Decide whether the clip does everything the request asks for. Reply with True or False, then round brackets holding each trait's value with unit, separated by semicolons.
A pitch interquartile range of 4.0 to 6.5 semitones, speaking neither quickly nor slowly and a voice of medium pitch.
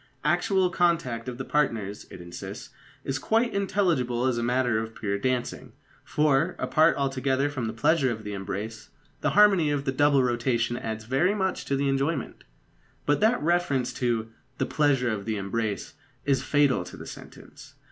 False (4.7 semitones; 165 wpm; 130 Hz)